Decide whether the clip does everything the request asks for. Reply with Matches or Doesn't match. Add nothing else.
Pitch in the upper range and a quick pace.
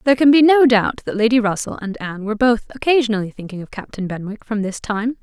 Matches